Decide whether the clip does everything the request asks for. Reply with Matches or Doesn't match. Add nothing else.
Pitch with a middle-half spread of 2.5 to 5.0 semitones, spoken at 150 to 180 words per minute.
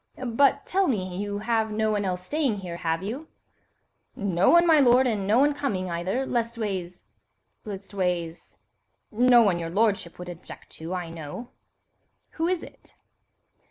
Doesn't match